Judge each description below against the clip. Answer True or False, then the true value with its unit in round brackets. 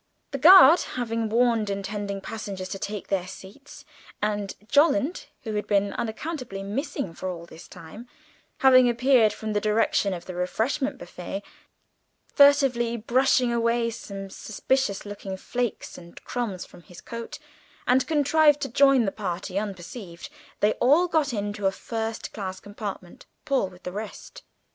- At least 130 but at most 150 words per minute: True (145 wpm)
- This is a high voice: True (220 Hz)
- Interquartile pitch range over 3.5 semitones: True (4.7 semitones)